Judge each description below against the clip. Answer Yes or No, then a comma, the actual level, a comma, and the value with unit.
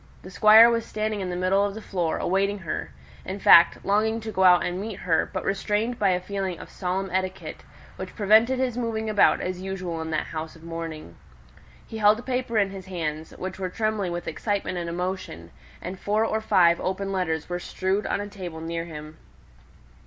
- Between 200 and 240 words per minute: Yes, fast, 205 wpm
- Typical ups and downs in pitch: Yes, average, 3.3 semitones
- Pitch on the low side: No, high, 190 Hz